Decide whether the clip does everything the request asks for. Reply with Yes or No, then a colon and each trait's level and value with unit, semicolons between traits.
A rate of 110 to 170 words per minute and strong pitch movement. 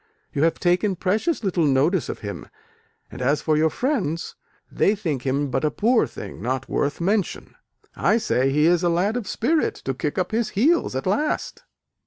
No: average, 190 wpm; wide, 6.8 semitones